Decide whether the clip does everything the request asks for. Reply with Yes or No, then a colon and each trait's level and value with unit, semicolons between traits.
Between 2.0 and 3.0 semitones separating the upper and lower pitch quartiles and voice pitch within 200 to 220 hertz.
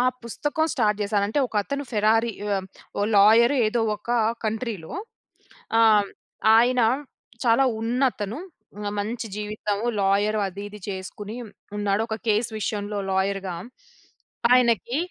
Yes: narrow, 2.5 semitones; high, 215 Hz